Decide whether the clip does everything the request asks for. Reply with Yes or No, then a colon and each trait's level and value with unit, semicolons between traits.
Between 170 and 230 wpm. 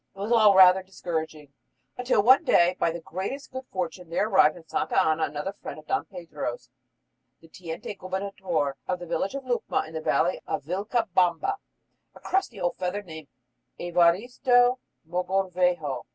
No: average, 160 wpm